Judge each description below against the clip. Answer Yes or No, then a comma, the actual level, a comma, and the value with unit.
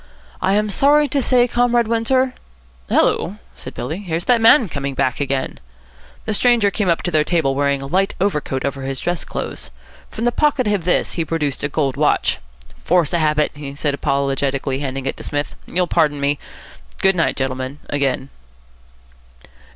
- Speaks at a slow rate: No, average, 180 wpm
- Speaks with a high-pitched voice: No, medium, 155 Hz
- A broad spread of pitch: Yes, wide, 6.9 semitones